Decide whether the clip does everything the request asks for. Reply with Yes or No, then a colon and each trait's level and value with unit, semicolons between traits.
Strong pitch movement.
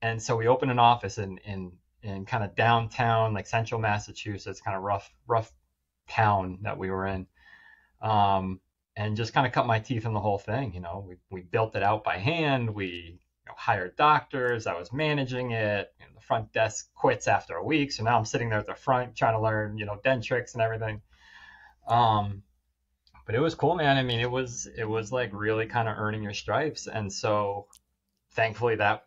No: average, 3.4 semitones